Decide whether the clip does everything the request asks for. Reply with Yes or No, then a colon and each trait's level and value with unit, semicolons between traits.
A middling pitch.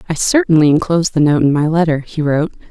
Yes: medium, 160 Hz